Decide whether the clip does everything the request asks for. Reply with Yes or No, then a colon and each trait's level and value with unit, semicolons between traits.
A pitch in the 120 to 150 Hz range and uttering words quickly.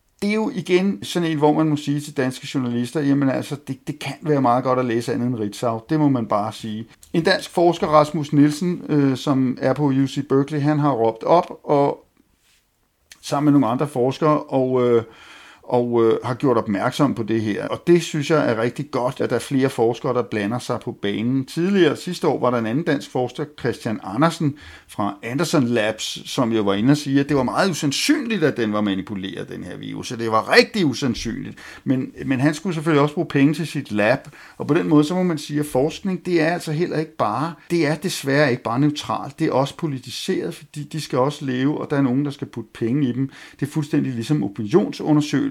Yes: medium, 140 Hz; fast, 230 wpm